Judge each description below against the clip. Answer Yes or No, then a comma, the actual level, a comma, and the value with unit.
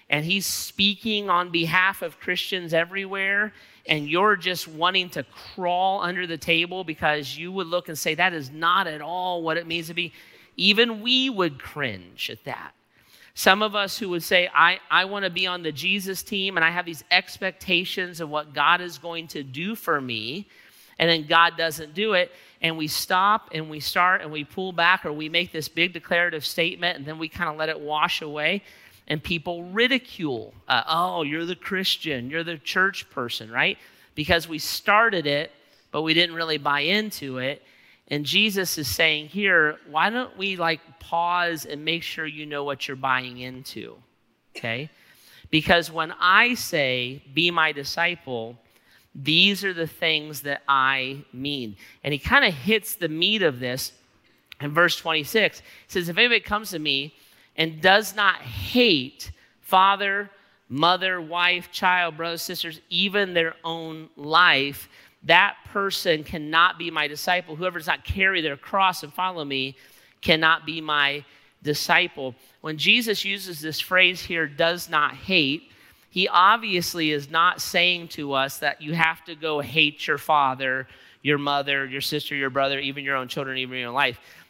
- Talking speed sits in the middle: Yes, average, 175 wpm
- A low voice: No, medium, 165 Hz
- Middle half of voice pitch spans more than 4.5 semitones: No, average, 3.8 semitones